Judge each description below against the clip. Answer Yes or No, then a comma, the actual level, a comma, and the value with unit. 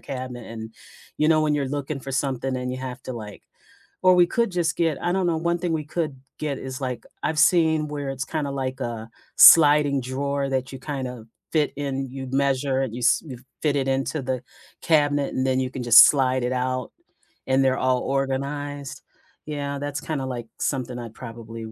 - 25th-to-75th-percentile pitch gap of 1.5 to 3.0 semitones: Yes, narrow, 2.5 semitones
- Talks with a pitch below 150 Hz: Yes, low, 135 Hz